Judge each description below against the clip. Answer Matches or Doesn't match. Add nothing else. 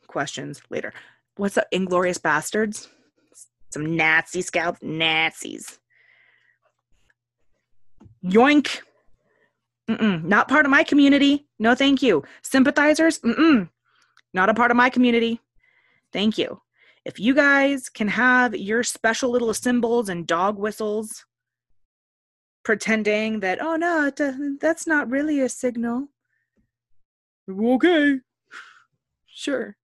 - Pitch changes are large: Matches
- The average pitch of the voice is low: Doesn't match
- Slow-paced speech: Matches